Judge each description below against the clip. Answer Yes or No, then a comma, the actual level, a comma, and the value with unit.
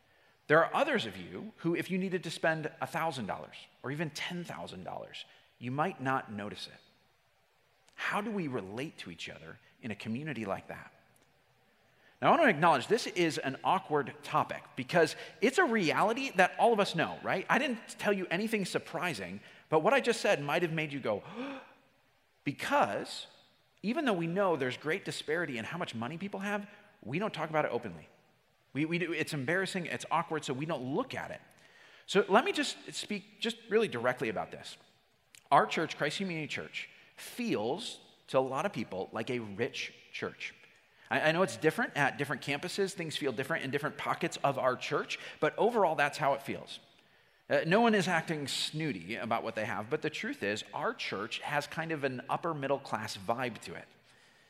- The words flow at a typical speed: Yes, average, 195 wpm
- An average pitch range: No, wide, 5.8 semitones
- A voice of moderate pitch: Yes, medium, 160 Hz